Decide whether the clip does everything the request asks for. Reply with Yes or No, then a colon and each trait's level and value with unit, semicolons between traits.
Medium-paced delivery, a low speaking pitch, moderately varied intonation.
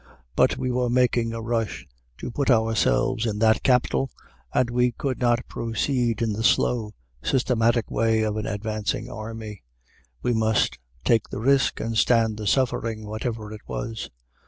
No: average, 155 wpm; low, 115 Hz; narrow, 2.0 semitones